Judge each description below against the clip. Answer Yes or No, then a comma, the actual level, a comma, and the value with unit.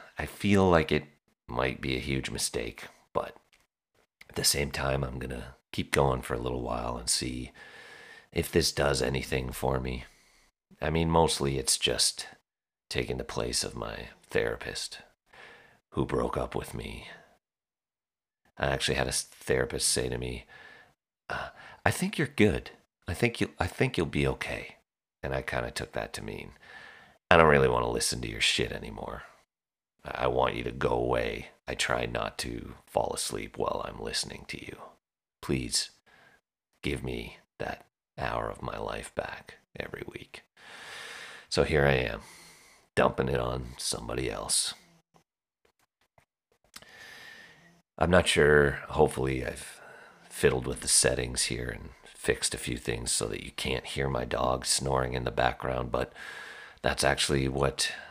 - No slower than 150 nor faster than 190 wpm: Yes, average, 155 wpm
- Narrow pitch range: Yes, narrow, 2.2 semitones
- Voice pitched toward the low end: Yes, very low, 65 Hz